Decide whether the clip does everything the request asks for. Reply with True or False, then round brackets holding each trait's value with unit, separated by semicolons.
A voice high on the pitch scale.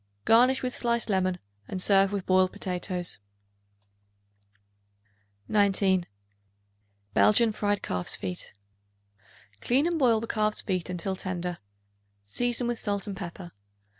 True (195 Hz)